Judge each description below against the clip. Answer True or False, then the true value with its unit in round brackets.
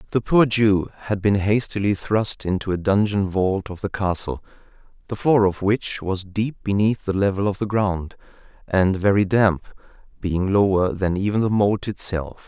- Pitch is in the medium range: False (100 Hz)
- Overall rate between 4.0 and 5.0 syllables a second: True (4.6 syllables/s)